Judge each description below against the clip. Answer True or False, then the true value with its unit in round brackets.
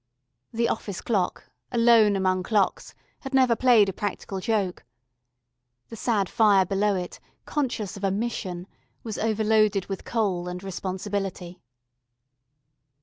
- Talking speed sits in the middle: False (125 wpm)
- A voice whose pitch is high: True (205 Hz)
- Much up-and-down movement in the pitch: False (3.0 semitones)